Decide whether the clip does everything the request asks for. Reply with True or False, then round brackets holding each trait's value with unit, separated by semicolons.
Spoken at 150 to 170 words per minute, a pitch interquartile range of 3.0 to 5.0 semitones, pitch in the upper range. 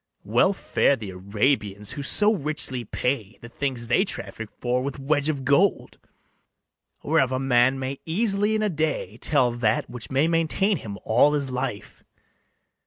False (160 wpm; 4.7 semitones; 135 Hz)